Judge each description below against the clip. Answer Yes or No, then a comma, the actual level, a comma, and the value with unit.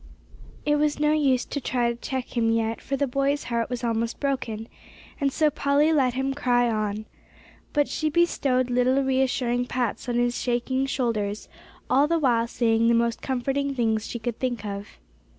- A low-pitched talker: No, very high, 250 Hz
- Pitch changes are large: No, average, 2.9 semitones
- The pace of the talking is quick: No, average, 180 wpm